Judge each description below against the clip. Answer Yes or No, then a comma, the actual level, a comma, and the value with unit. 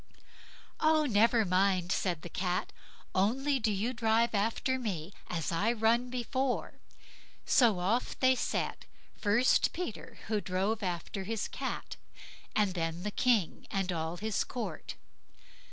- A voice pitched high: Yes, high, 210 Hz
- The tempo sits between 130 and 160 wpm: Yes, slow, 135 wpm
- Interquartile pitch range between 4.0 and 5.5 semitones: Yes, average, 4.5 semitones